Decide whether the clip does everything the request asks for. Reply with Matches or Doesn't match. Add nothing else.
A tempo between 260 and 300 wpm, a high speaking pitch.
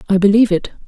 Doesn't match